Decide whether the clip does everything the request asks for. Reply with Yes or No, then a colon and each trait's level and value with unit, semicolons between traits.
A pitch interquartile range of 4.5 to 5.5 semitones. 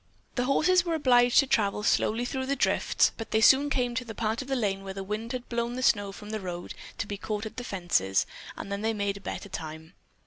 No: average, 3.9 semitones